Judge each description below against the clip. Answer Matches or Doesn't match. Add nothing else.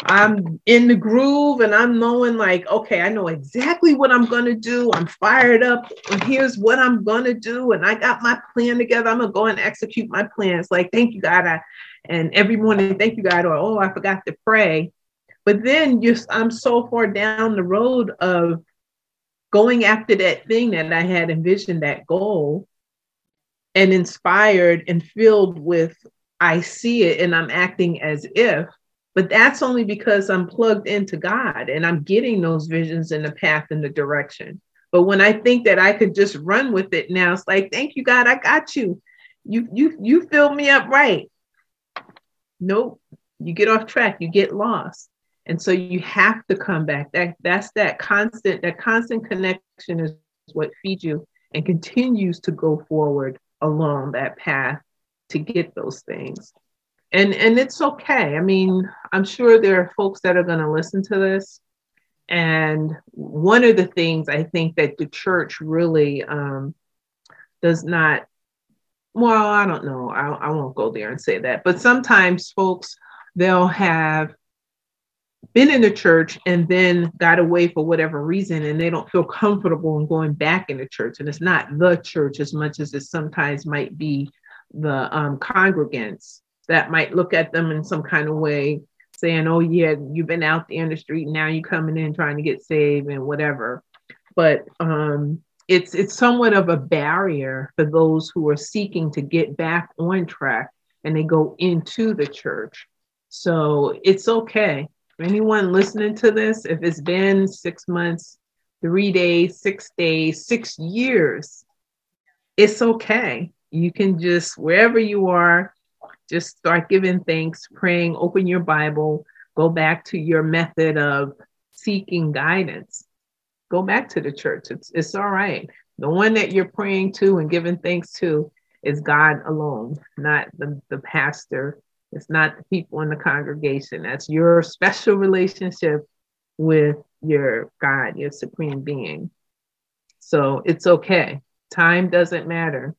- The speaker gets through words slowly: Doesn't match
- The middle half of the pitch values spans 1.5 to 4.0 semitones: Doesn't match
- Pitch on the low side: Doesn't match